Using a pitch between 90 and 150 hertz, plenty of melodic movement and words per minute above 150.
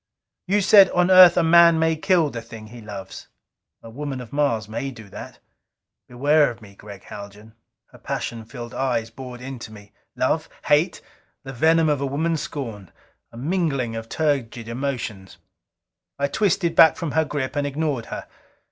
Yes: low, 135 Hz; wide, 5.8 semitones; average, 170 wpm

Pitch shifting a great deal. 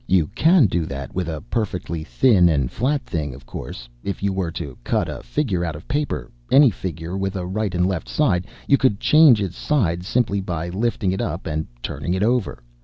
Yes: wide, 5.7 semitones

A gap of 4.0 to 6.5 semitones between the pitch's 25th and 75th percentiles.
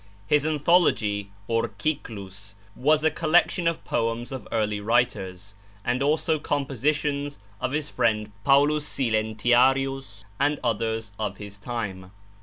Yes: average, 5.3 semitones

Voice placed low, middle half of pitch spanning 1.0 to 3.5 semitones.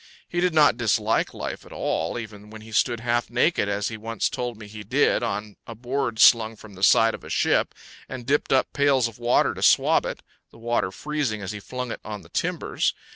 Yes: low, 115 Hz; average, 2.9 semitones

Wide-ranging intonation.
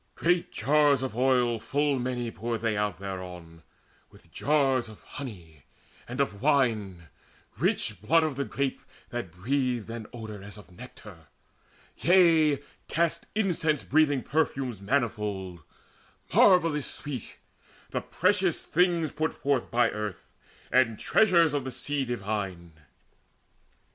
Yes: wide, 6.0 semitones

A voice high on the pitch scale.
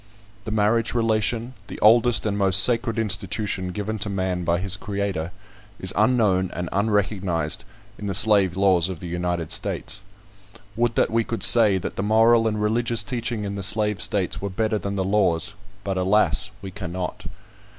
No: low, 100 Hz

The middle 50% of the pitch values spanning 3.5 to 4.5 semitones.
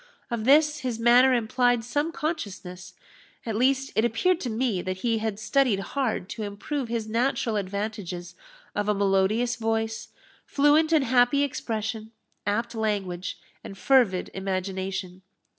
Yes: average, 4.1 semitones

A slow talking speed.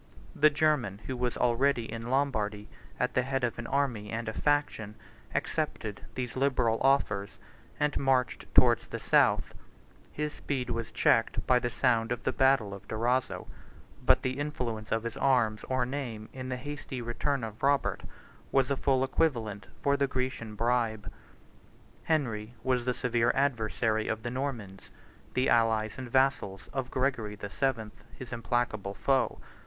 No: average, 160 wpm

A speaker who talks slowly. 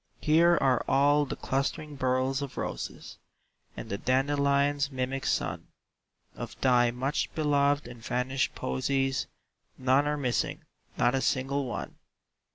Yes: slow, 130 wpm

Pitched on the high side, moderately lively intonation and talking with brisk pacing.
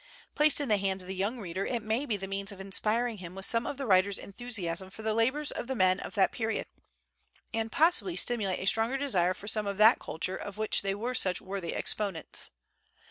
Yes: high, 210 Hz; average, 3.7 semitones; fast, 225 wpm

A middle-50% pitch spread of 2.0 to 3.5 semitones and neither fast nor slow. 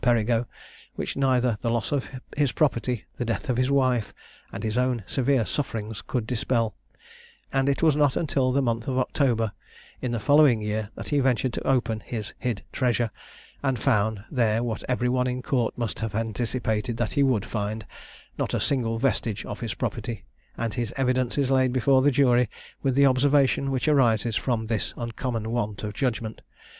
Yes: average, 2.7 semitones; average, 185 wpm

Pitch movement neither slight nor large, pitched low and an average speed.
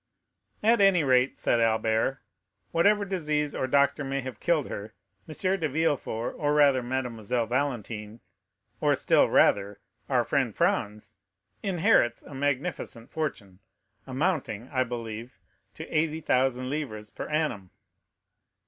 No: average, 5.0 semitones; low, 130 Hz; slow, 120 wpm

